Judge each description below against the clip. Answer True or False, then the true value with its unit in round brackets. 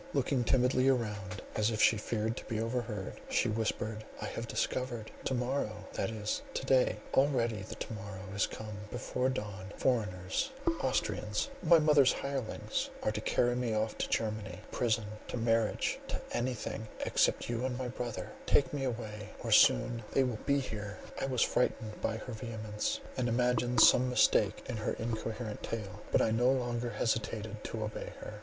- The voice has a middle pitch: False (115 Hz)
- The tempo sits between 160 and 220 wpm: True (165 wpm)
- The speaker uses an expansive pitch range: False (2.7 semitones)